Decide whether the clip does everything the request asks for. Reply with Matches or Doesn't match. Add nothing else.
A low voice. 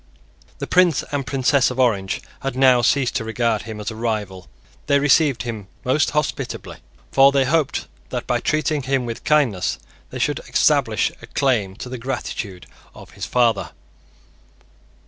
Matches